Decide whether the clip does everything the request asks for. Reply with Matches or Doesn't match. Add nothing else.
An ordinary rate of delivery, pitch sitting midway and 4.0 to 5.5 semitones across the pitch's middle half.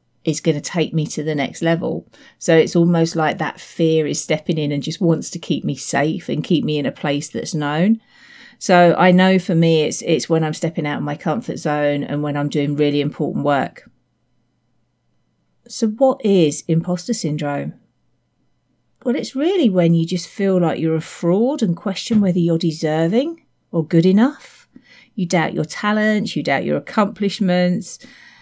Matches